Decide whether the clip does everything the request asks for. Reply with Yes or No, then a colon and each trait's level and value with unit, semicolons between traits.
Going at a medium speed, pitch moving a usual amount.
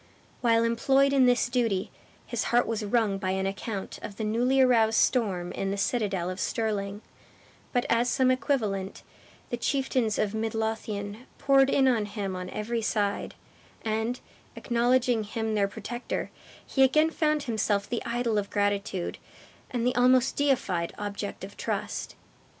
Yes: average, 155 wpm; average, 3.5 semitones